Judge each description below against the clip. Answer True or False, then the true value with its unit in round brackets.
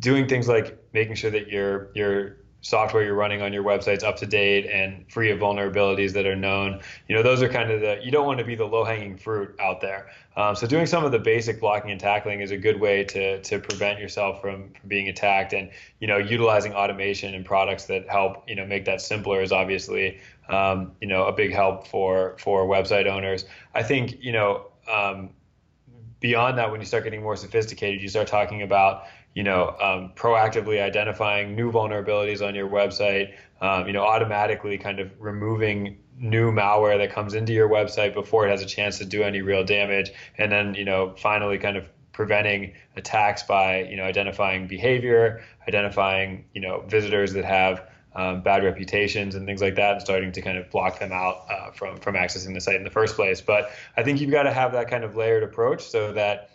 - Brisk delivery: True (210 wpm)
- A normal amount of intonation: False (2.0 semitones)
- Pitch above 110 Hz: False (100 Hz)